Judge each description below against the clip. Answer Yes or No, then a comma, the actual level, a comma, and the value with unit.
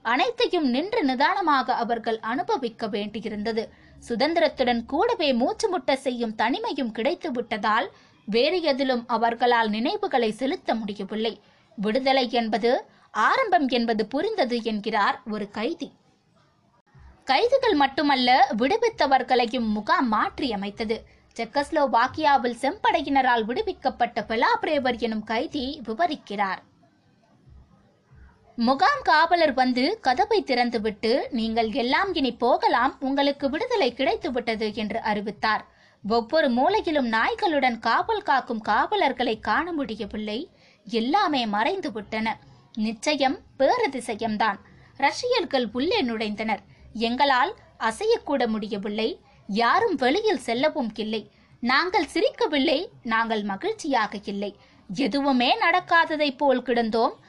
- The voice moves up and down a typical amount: Yes, average, 4.9 semitones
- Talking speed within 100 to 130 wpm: No, average, 90 wpm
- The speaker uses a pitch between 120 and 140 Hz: No, very high, 255 Hz